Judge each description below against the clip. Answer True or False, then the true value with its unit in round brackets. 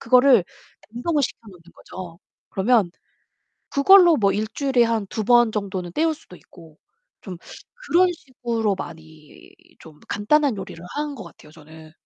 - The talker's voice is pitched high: True (220 Hz)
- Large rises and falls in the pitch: True (7.4 semitones)